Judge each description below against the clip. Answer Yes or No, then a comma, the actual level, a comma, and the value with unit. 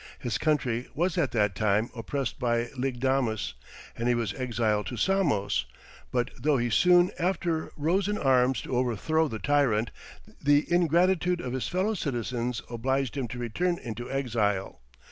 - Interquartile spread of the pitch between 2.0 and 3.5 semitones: No, average, 5.3 semitones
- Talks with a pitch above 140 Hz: No, low, 125 Hz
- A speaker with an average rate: Yes, average, 155 wpm